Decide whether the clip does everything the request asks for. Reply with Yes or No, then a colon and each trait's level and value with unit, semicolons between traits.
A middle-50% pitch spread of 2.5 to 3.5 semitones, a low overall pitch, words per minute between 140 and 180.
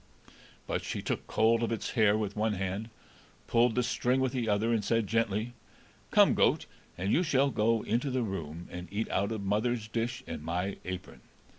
No: average, 3.0 semitones; low, 110 Hz; average, 190 wpm